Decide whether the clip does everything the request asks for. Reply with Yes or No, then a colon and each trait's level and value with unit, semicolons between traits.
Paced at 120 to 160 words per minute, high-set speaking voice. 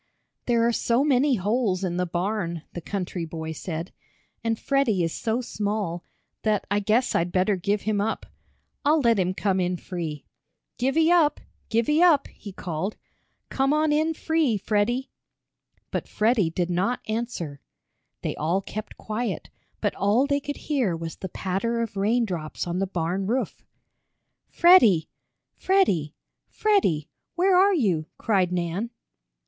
Yes: average, 150 wpm; high, 210 Hz